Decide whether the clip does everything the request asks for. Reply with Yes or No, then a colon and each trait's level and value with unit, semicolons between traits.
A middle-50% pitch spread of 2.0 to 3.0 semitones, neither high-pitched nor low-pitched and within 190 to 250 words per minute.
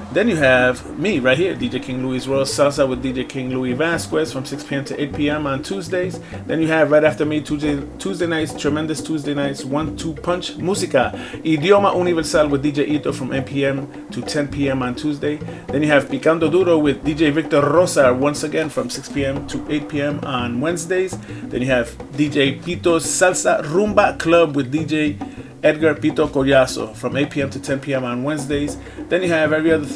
Yes: narrow, 2.5 semitones; medium, 150 Hz; average, 200 wpm